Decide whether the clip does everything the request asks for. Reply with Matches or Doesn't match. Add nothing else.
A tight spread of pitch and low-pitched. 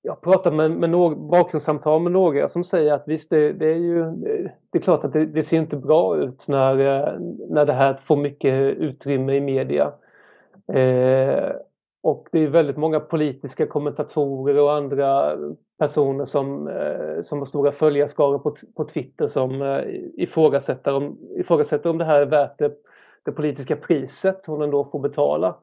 Doesn't match